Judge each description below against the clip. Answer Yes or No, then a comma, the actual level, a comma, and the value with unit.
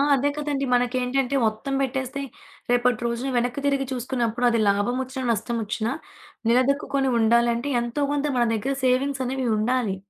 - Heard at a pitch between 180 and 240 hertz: No, very high, 250 Hz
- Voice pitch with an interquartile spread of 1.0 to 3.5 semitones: Yes, narrow, 2.4 semitones